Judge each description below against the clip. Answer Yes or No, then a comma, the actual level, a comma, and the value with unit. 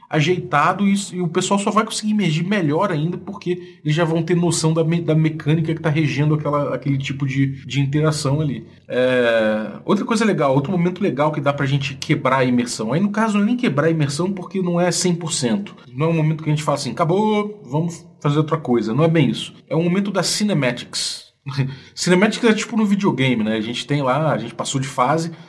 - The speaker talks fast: Yes, fast, 215 wpm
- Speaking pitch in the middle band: Yes, medium, 160 Hz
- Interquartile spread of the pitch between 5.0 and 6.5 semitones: No, average, 4.5 semitones